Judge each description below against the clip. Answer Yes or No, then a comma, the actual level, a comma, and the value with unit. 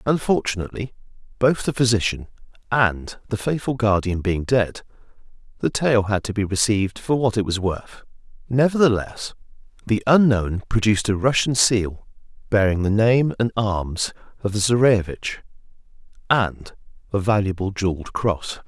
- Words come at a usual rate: No, slow, 130 wpm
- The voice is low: Yes, low, 110 Hz